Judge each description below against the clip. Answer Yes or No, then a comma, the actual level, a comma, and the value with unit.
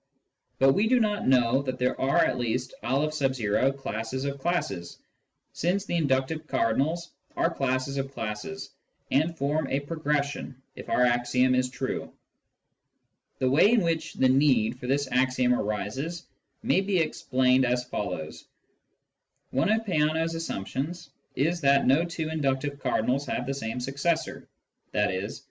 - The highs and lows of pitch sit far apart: No, average, 3.9 semitones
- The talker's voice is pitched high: No, low, 135 Hz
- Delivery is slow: No, average, 145 wpm